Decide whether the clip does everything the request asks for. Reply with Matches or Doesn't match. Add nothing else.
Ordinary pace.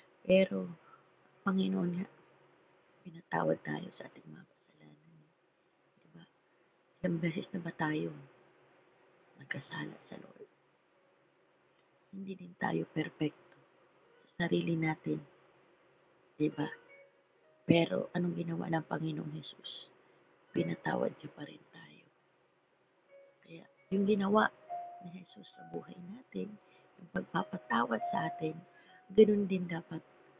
Doesn't match